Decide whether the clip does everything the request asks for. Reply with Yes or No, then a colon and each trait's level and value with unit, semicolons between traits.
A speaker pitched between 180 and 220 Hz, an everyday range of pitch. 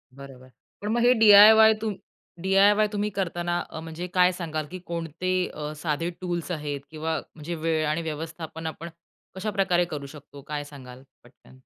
No: medium, 165 Hz; average, 3.6 semitones